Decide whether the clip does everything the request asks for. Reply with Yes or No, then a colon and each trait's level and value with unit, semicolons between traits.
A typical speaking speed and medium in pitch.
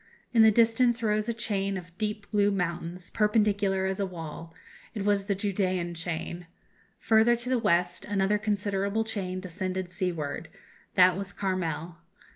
No: average, 150 wpm; high, 195 Hz